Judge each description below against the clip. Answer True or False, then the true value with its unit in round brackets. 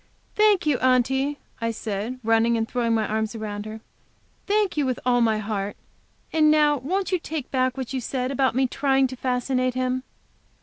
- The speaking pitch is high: True (255 Hz)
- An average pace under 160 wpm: False (185 wpm)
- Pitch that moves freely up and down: False (3.3 semitones)